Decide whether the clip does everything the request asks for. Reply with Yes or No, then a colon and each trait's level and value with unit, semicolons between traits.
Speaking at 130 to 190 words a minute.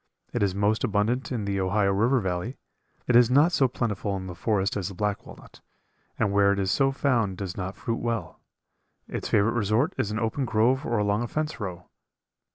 No: fast, 205 wpm